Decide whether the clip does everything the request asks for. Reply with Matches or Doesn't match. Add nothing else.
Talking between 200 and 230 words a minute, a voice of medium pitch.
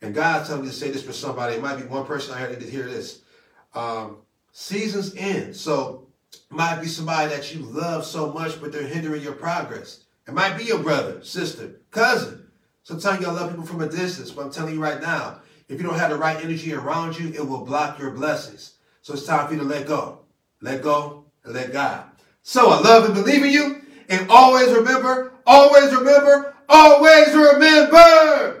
Matches